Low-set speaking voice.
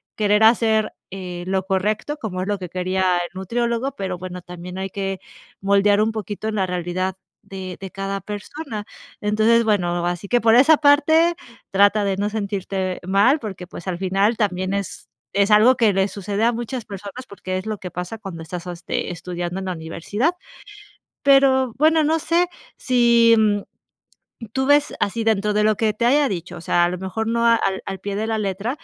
No: high, 205 Hz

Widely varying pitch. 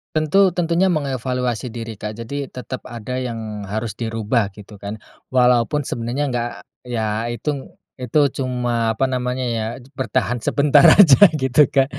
No: average, 3.1 semitones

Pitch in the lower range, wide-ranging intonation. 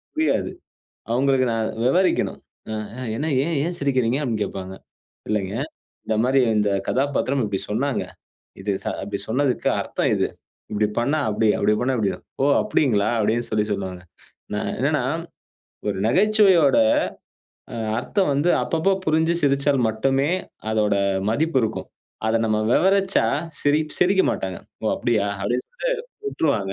Yes: low, 125 Hz; wide, 6.0 semitones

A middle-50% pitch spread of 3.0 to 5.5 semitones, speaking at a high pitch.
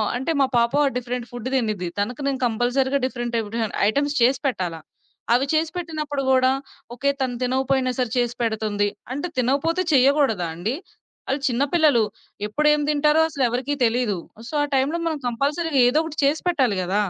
Yes: average, 3.6 semitones; very high, 260 Hz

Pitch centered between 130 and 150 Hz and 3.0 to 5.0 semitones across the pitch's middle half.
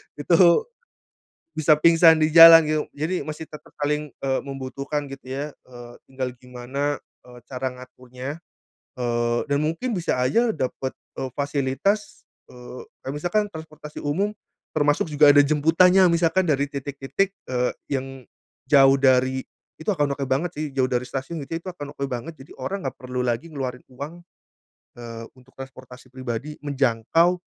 Yes: medium, 140 Hz; average, 3.7 semitones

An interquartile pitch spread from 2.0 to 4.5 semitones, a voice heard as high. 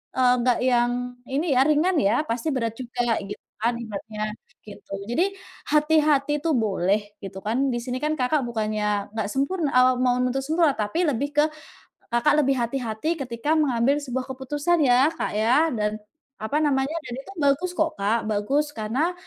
No: average, 5.0 semitones; very high, 255 Hz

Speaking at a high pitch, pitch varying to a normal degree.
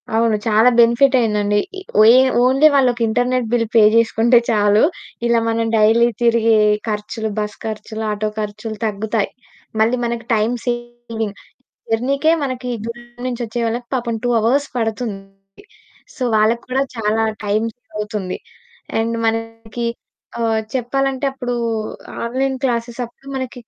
No: high, 230 Hz; narrow, 2.0 semitones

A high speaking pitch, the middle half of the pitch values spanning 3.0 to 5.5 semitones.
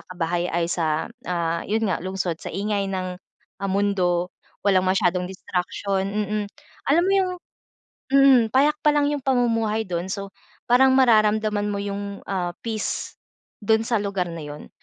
Yes: high, 200 Hz; average, 3.5 semitones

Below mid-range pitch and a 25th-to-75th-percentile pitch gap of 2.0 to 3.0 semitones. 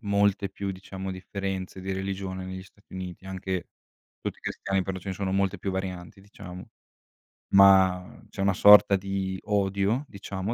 No: very low, 95 Hz; narrow, 0.9 semitones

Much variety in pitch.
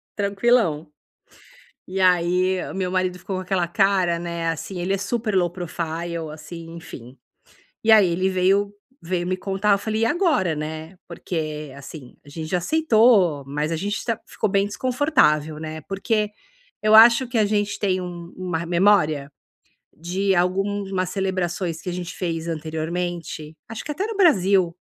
No: average, 3.4 semitones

